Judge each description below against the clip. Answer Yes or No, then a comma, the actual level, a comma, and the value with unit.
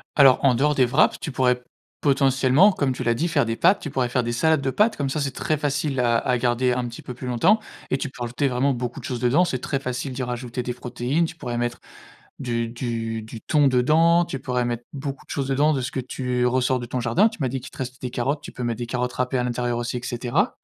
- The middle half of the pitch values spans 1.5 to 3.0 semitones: Yes, narrow, 2.4 semitones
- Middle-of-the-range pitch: No, low, 125 Hz